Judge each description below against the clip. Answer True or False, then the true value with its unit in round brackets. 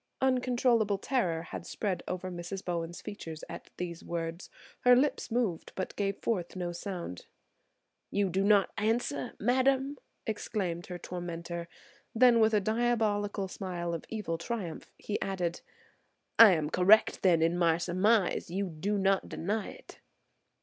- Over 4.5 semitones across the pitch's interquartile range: False (4.1 semitones)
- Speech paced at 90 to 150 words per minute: True (145 wpm)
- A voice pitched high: True (195 Hz)